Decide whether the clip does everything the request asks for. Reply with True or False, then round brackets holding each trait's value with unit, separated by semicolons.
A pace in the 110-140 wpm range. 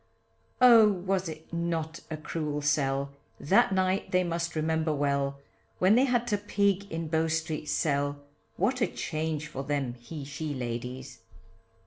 False (150 wpm)